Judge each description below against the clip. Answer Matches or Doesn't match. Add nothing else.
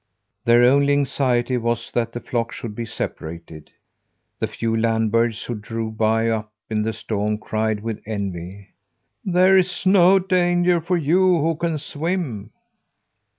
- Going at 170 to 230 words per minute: Doesn't match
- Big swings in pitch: Matches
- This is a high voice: Doesn't match